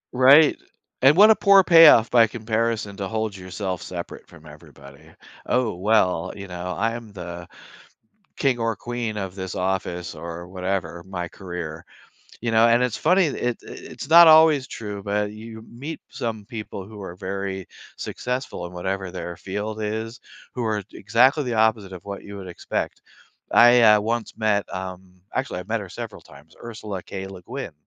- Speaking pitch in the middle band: No, low, 105 Hz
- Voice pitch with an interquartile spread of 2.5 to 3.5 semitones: No, average, 4.2 semitones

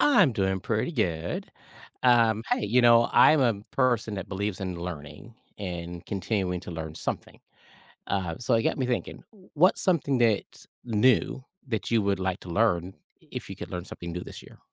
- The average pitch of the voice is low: Yes, low, 105 Hz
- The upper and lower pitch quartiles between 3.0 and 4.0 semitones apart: No, average, 4.8 semitones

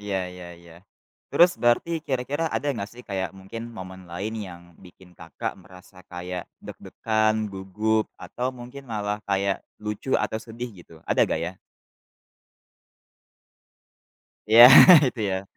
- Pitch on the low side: Yes, low, 105 Hz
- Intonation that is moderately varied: Yes, average, 4.1 semitones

